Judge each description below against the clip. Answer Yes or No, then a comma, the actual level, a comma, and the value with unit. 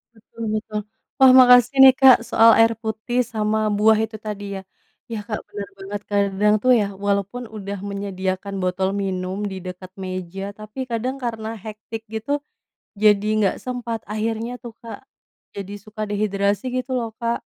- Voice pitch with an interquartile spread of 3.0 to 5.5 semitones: No, narrow, 2.4 semitones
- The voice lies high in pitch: Yes, high, 215 Hz